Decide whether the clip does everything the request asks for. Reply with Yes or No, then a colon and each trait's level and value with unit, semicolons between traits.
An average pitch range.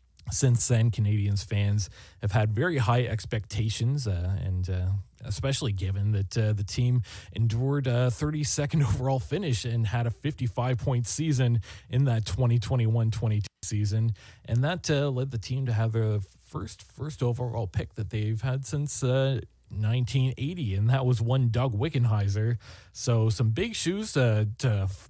Yes: average, 3.5 semitones